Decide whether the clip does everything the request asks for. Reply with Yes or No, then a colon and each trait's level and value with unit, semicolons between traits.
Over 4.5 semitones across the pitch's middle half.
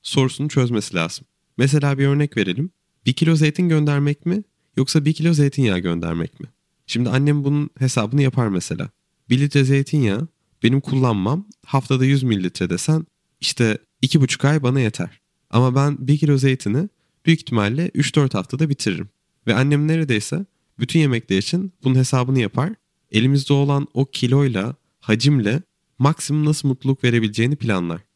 No: average, 3.8 semitones